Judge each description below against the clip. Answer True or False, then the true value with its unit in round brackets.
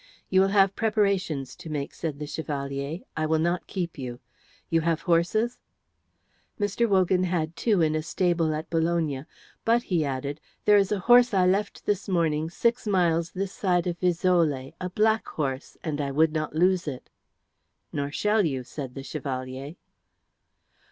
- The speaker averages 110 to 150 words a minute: False (165 wpm)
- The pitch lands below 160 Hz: False (170 Hz)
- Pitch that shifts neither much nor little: True (4.2 semitones)